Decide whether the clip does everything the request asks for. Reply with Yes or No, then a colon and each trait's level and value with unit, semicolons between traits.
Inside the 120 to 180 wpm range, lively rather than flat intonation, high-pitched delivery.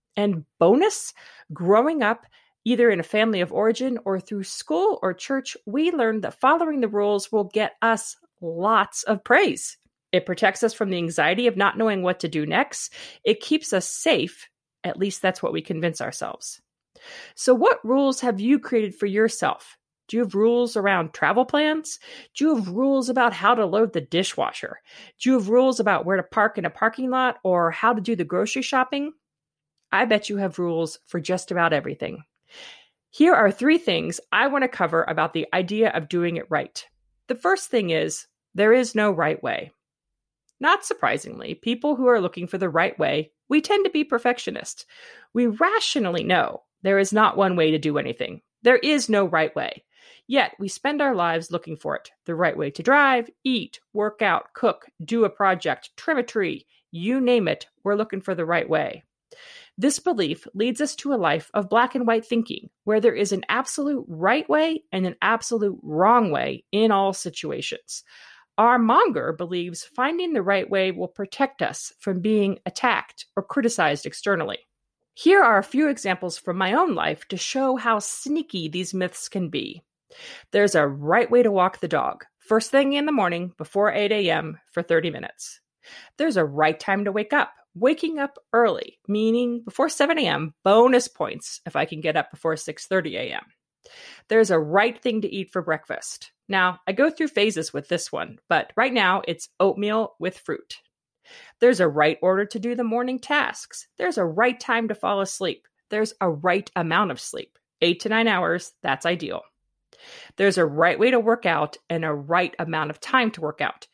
No: average, 190 wpm; wide, 6.2 semitones; high, 215 Hz